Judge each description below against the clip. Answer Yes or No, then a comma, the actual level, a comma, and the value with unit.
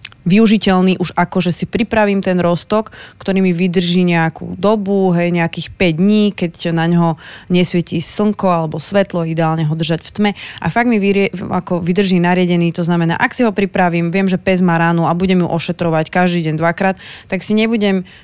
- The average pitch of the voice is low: No, medium, 180 Hz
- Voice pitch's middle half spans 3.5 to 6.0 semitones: No, average, 2.7 semitones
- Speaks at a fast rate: Yes, fast, 190 wpm